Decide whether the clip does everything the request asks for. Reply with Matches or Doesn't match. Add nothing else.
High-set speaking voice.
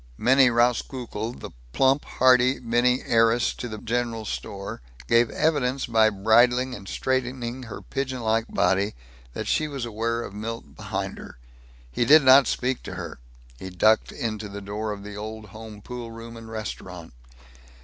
Doesn't match